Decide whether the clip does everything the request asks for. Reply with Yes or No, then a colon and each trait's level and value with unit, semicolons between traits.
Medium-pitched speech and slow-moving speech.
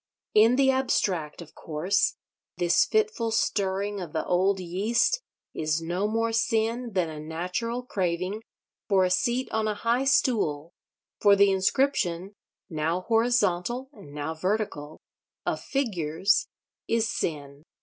No: high, 195 Hz; slow, 125 wpm